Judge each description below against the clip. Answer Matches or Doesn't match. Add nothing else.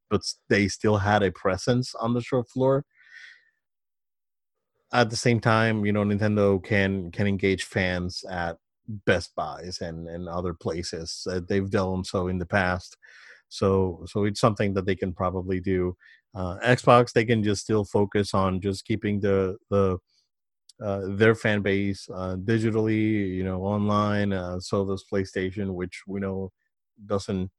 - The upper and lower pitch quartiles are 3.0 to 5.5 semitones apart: Doesn't match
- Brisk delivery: Doesn't match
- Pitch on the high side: Doesn't match